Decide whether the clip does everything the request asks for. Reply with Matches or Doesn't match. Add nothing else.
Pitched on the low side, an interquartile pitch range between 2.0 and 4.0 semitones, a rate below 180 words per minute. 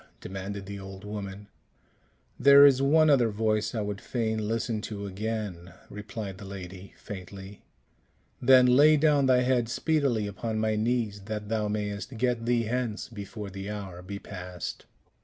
Matches